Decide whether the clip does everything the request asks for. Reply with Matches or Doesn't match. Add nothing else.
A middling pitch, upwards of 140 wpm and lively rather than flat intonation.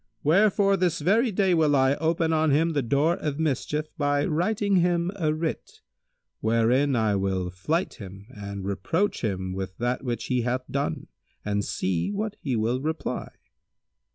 Matches